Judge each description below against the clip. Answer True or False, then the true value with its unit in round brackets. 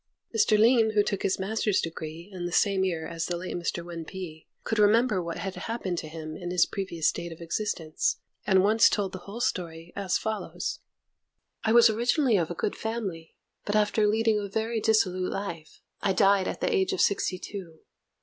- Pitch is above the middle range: True (195 Hz)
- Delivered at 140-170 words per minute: False (200 wpm)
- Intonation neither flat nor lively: True (4.1 semitones)